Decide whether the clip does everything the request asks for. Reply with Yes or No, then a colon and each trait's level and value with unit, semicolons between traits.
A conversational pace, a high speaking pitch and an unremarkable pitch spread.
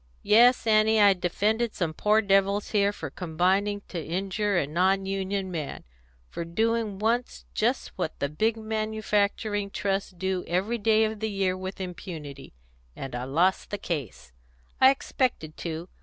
Yes: average, 155 wpm; high, 195 Hz; average, 3.7 semitones